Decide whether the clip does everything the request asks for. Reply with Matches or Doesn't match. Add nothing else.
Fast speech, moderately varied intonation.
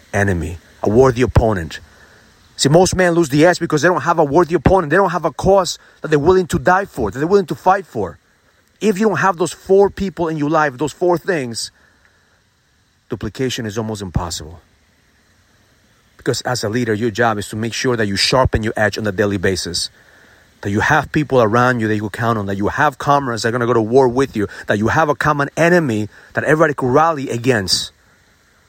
Doesn't match